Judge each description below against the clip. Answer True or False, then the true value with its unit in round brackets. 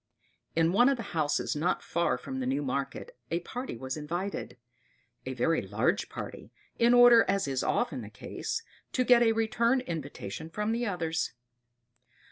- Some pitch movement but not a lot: False (8.0 semitones)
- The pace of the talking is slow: False (165 wpm)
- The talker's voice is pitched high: False (175 Hz)